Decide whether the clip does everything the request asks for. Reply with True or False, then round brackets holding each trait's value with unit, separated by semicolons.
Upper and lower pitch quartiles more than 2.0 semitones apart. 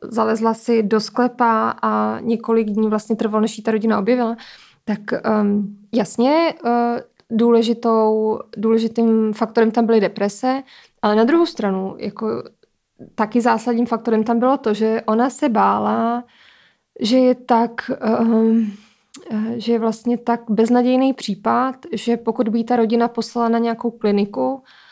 False (1.5 semitones)